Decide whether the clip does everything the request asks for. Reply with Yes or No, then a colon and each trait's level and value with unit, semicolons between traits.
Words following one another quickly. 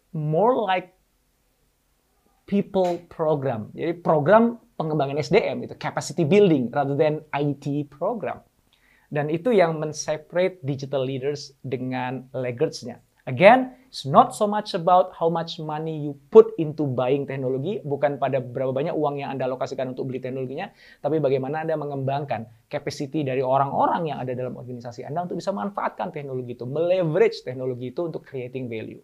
Yes: fast, 150 wpm